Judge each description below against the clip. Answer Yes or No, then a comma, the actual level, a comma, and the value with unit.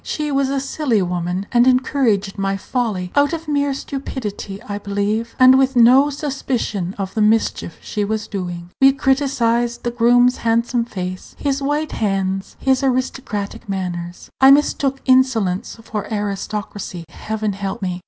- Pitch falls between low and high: No, high, 230 Hz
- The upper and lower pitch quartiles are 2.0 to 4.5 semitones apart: No, average, 5.3 semitones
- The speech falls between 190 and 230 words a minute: No, average, 150 wpm